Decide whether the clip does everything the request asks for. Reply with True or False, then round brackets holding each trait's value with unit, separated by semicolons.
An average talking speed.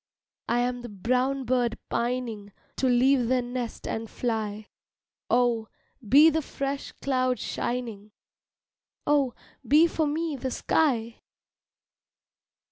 False (115 wpm)